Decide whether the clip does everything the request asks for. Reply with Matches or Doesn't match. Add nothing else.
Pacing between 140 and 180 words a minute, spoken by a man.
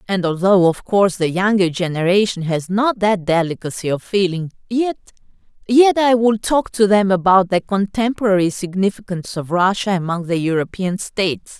Doesn't match